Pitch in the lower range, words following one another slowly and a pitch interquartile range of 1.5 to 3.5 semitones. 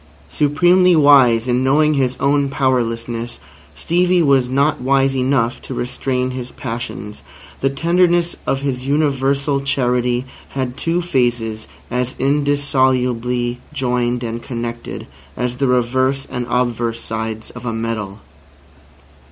Yes: low, 130 Hz; slow, 120 wpm; narrow, 2.5 semitones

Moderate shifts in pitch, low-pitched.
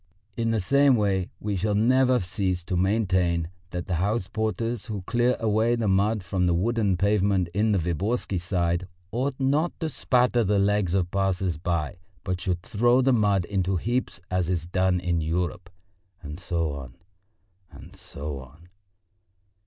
Yes: average, 4.1 semitones; very low, 95 Hz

